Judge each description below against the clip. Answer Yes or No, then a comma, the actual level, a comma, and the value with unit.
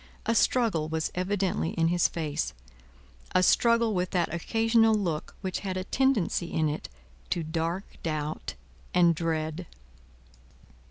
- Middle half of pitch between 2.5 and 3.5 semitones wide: No, average, 4.1 semitones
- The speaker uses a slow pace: Yes, slow, 130 wpm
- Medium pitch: Yes, medium, 175 Hz